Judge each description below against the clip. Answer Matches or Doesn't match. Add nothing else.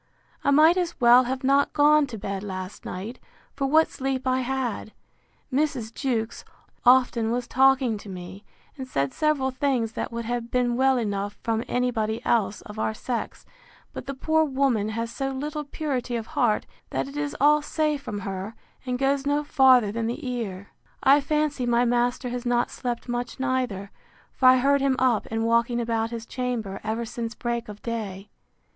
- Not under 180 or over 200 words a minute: Matches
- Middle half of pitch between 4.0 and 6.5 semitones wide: Doesn't match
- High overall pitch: Matches